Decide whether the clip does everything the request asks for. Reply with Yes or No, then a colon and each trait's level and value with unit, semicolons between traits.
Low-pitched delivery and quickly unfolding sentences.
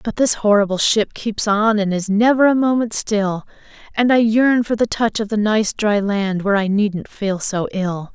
No: high, 210 Hz; fast, 215 wpm